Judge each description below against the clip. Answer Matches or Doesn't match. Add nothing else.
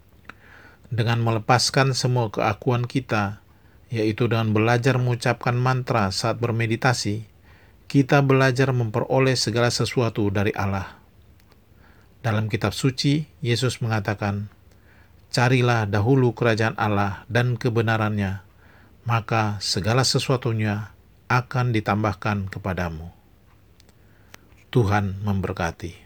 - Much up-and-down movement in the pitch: Doesn't match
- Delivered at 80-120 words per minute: Matches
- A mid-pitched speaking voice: Doesn't match